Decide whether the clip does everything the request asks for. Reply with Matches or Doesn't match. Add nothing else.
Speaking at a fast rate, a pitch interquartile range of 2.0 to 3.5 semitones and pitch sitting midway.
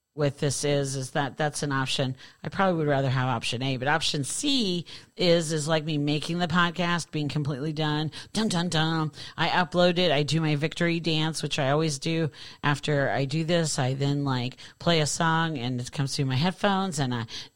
Matches